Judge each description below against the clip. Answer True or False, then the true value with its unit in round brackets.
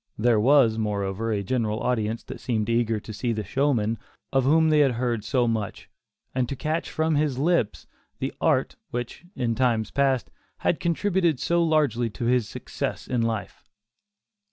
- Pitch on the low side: True (120 Hz)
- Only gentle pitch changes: False (4.4 semitones)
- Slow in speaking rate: False (170 wpm)